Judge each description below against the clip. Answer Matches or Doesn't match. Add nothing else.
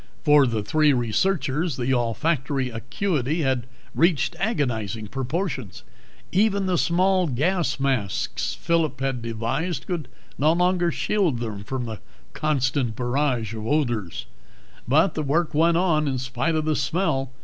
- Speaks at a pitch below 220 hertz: Matches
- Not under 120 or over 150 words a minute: Matches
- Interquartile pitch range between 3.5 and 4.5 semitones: Doesn't match